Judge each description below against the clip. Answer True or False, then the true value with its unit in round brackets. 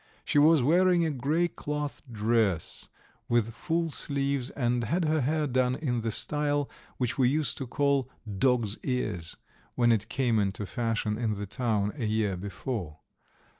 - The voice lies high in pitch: False (125 Hz)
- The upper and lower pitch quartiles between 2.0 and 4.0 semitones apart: False (4.9 semitones)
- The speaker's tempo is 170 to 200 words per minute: False (160 wpm)